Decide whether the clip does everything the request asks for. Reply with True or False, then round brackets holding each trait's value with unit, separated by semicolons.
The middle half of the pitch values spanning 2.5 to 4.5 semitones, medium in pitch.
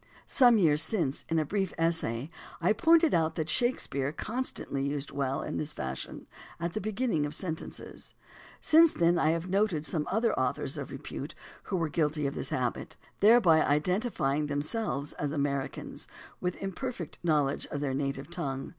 False (5.3 semitones; 160 Hz)